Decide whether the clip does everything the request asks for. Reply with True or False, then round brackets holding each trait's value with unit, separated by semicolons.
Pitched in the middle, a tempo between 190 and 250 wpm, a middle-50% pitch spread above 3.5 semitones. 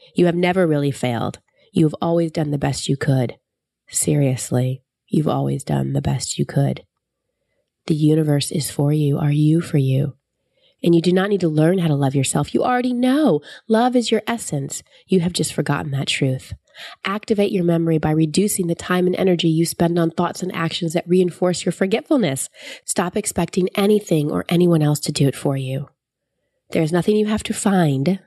True (165 Hz; 195 wpm; 4.4 semitones)